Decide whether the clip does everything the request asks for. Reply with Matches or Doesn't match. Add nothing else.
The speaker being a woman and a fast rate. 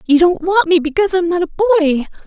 Matches